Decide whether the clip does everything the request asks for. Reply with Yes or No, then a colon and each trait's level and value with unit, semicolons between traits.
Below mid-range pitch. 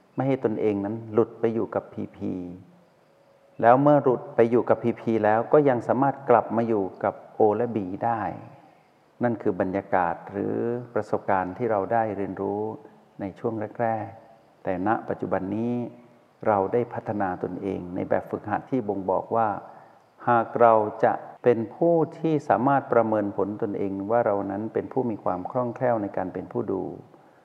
Yes: low, 115 Hz